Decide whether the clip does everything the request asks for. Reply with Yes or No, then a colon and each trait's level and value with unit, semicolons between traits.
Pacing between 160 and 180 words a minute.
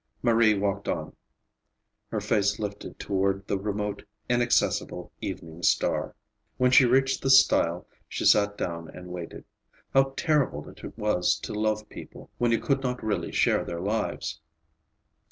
No: average, 145 wpm